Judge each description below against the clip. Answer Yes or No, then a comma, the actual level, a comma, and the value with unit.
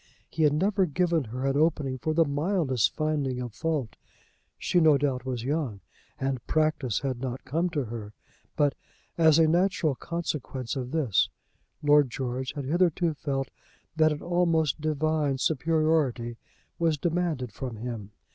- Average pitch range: Yes, average, 3.8 semitones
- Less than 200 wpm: Yes, average, 150 wpm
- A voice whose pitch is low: No, medium, 145 Hz